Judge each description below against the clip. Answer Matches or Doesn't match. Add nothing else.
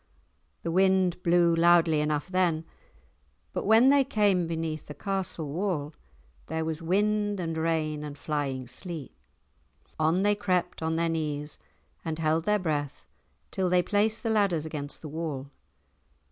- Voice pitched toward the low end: Doesn't match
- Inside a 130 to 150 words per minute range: Matches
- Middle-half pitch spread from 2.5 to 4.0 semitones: Matches